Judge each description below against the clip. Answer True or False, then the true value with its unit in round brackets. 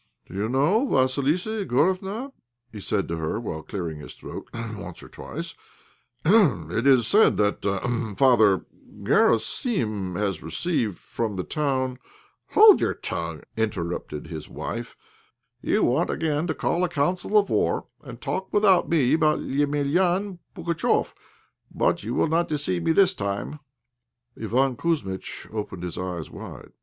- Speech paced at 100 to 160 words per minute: True (145 wpm)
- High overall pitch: False (130 Hz)